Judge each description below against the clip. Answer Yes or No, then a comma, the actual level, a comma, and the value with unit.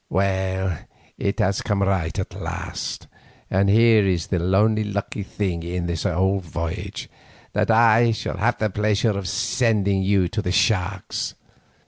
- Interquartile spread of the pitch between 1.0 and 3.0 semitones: Yes, narrow, 2.4 semitones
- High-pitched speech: No, low, 100 Hz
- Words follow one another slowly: No, average, 150 wpm